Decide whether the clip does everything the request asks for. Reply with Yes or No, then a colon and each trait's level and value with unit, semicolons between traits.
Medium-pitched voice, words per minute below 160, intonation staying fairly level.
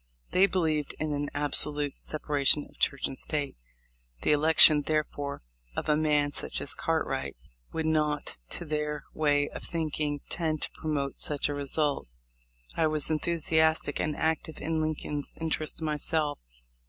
Yes: medium, 150 Hz; average, 145 wpm; narrow, 1.4 semitones